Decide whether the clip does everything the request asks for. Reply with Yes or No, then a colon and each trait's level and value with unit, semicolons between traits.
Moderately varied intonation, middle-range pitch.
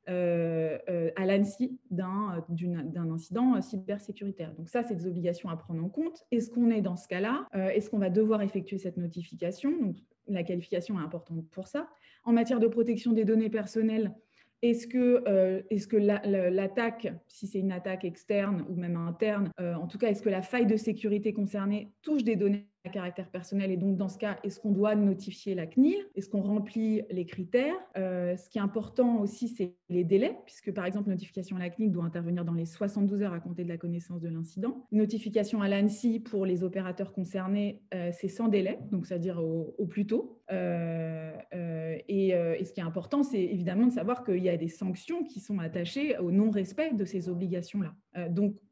No: average, 3.3 semitones; high, 195 Hz